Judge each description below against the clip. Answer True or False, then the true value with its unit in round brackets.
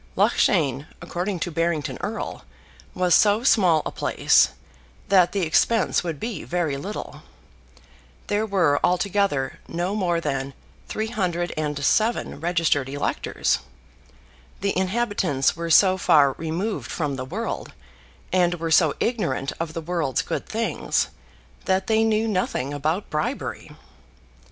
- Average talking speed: False (120 wpm)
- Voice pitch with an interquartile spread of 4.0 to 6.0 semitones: True (4.6 semitones)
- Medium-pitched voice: True (175 Hz)